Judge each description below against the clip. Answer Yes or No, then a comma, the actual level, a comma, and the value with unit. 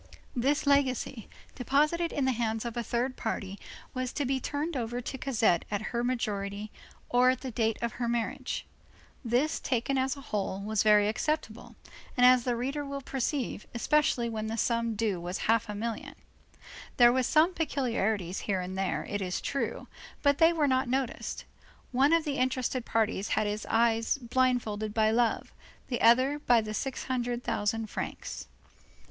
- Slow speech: No, average, 170 wpm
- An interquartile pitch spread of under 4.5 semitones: Yes, average, 3.4 semitones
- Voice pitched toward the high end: Yes, high, 240 Hz